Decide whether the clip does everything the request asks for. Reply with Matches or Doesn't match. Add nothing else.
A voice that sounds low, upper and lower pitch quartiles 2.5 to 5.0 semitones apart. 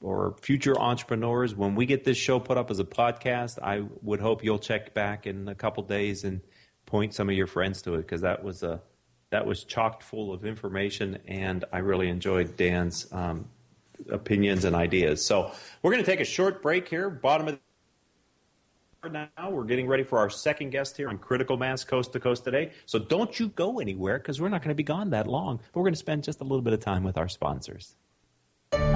Doesn't match